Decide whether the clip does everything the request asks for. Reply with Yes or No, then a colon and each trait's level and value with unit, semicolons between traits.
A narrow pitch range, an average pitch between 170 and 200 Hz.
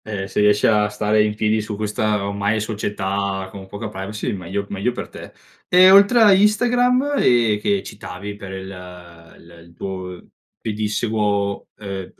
No: narrow, 2.1 semitones; low, 105 Hz